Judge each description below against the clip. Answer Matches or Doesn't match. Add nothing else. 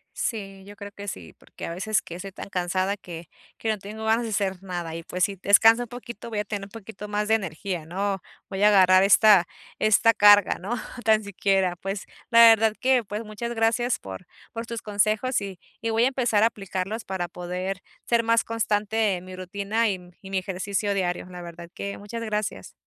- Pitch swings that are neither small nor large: Matches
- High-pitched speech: Matches